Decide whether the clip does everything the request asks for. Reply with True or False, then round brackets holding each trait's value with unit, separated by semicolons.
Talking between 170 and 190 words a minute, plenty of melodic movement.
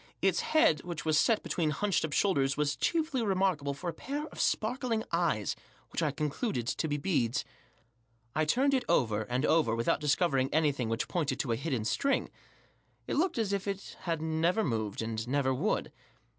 True (185 wpm; 6.7 semitones)